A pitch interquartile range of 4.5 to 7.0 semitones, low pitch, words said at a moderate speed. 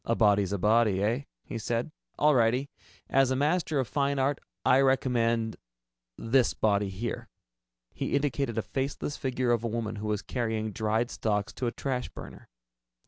No: average, 3.5 semitones; low, 115 Hz; average, 170 wpm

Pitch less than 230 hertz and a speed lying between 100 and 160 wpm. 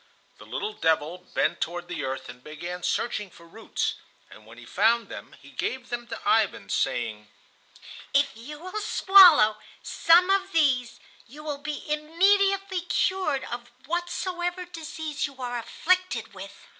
No: very high, 280 Hz; average, 150 wpm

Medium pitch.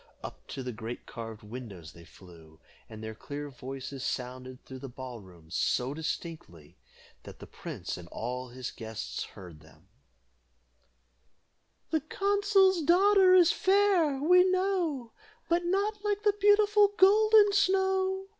Yes: medium, 165 Hz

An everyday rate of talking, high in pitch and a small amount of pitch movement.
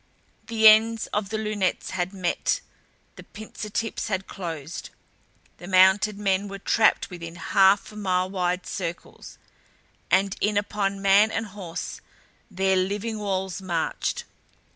No: slow, 130 wpm; high, 195 Hz; narrow, 2.3 semitones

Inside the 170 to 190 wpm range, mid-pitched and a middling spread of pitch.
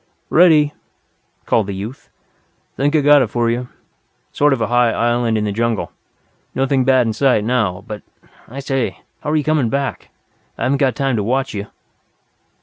No: average, 175 wpm; low, 125 Hz; average, 3.5 semitones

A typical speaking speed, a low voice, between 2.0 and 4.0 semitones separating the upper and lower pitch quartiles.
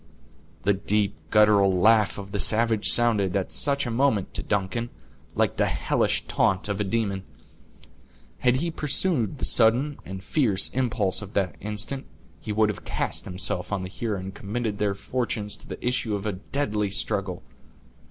Yes: average, 170 wpm; low, 105 Hz; average, 3.2 semitones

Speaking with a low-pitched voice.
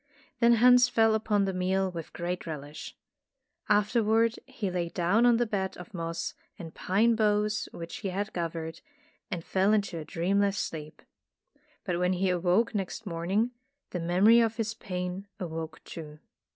No: high, 190 Hz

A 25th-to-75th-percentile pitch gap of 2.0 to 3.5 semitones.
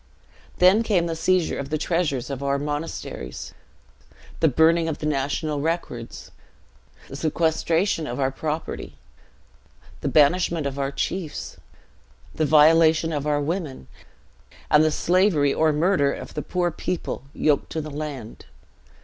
Yes: average, 2.7 semitones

